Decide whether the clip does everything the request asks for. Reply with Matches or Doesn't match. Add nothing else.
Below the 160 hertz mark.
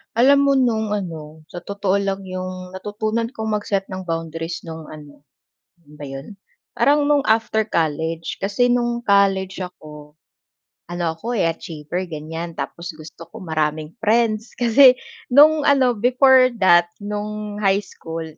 Doesn't match